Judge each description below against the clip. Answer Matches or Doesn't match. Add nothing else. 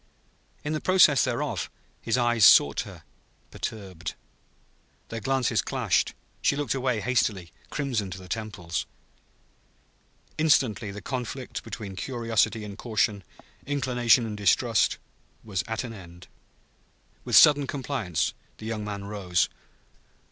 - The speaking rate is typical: Doesn't match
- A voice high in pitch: Doesn't match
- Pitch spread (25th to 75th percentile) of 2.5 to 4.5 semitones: Matches